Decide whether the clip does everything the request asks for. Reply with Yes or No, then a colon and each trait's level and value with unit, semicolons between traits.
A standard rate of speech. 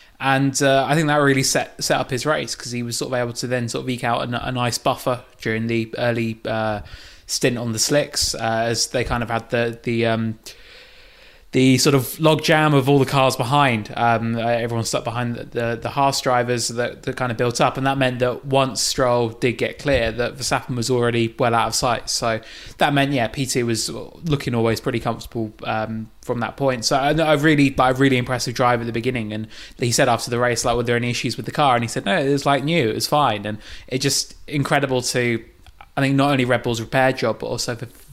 No: fast, 240 wpm